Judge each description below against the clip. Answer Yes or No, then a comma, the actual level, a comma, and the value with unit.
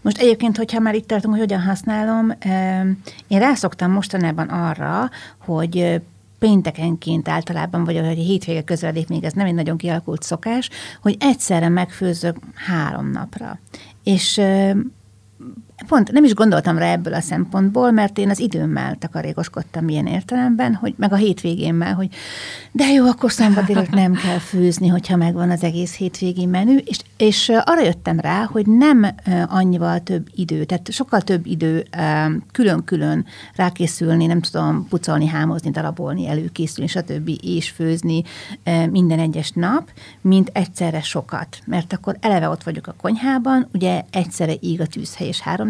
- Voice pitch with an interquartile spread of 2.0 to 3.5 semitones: No, average, 4.2 semitones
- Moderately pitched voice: Yes, medium, 180 Hz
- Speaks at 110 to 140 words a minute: No, average, 150 wpm